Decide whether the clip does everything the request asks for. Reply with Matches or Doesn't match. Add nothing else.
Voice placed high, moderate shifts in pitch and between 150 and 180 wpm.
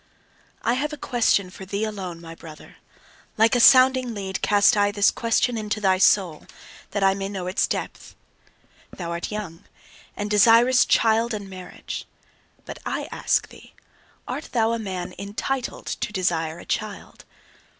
Matches